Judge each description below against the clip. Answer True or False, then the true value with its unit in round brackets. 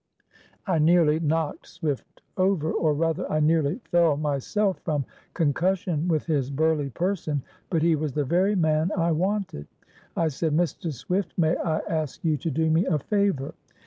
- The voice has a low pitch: False (160 Hz)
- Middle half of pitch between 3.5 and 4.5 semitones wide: False (2.7 semitones)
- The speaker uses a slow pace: False (165 wpm)